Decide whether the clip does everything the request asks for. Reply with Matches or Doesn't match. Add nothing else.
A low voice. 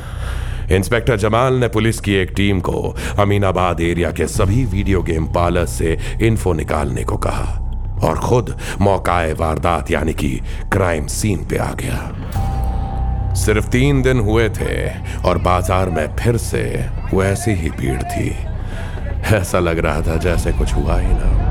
Matches